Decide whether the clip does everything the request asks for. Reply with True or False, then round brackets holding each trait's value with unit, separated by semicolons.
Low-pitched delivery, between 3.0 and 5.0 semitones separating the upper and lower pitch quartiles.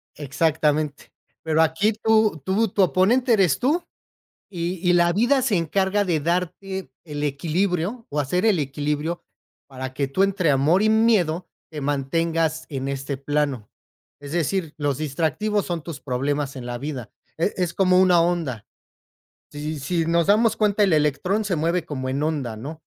False (165 Hz; 4.7 semitones)